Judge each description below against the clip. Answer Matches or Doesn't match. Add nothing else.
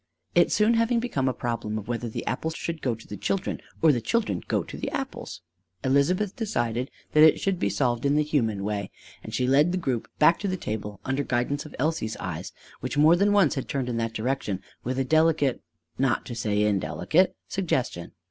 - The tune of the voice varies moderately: Doesn't match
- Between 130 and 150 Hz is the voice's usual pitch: Matches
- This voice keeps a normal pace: Doesn't match